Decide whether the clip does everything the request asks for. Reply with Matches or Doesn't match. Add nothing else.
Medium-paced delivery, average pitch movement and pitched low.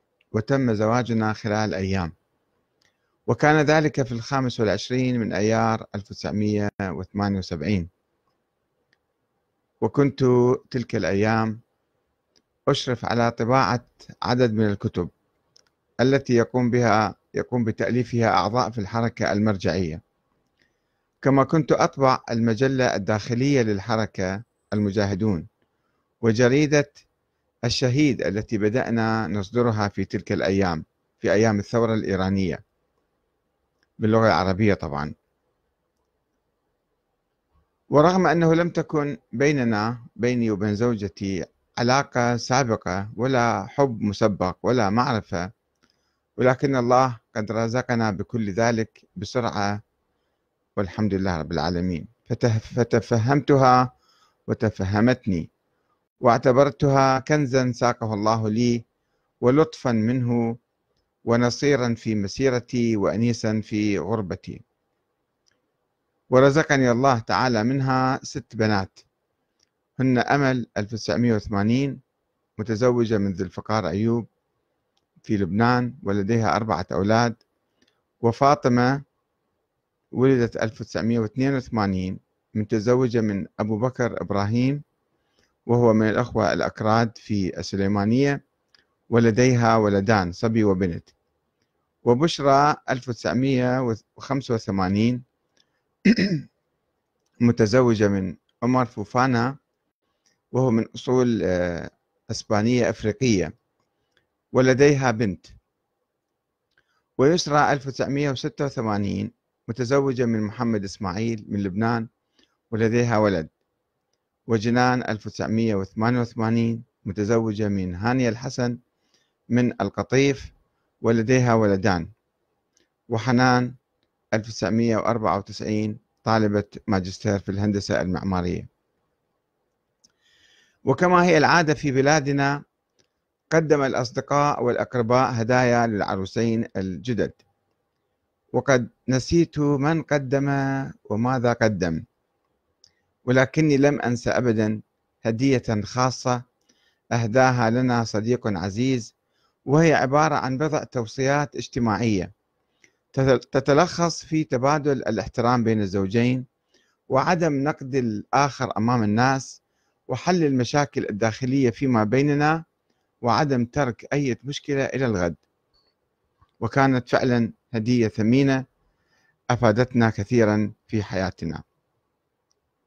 Matches